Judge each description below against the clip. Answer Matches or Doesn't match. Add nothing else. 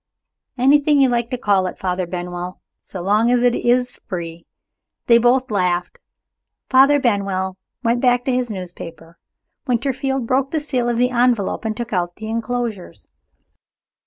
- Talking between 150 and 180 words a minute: Matches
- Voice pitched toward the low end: Doesn't match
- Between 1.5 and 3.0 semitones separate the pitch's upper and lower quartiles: Doesn't match